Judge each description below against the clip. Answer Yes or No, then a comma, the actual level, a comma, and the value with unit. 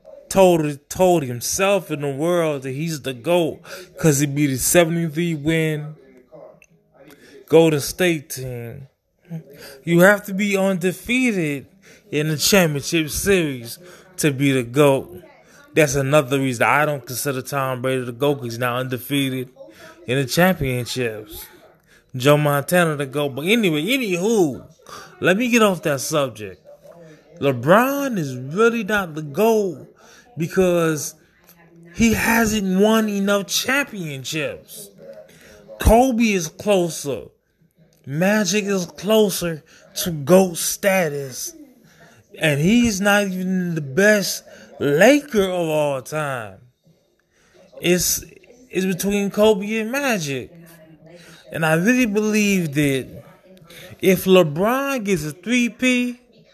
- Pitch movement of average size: No, wide, 5.7 semitones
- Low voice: No, medium, 170 Hz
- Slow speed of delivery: Yes, slow, 115 wpm